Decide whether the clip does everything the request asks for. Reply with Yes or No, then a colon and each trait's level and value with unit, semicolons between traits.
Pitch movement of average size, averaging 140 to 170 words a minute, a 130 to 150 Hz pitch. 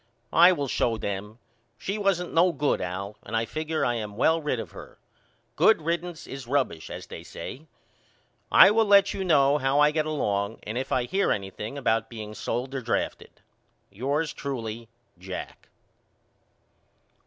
No: wide, 6.3 semitones; average, 165 wpm; low, 135 Hz